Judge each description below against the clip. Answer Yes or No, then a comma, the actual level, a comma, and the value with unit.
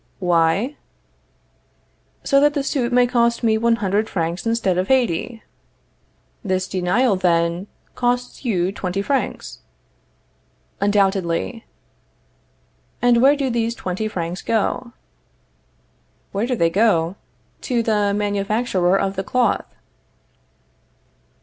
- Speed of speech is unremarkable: No, slow, 110 wpm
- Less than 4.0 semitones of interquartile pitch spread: No, average, 4.5 semitones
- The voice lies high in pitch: Yes, high, 205 Hz